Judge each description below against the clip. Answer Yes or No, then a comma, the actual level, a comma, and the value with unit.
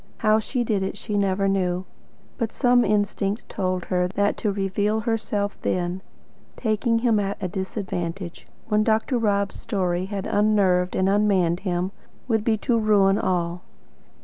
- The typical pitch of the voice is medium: No, high, 200 Hz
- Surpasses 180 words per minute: No, average, 150 wpm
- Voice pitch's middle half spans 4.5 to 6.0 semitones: No, narrow, 2.6 semitones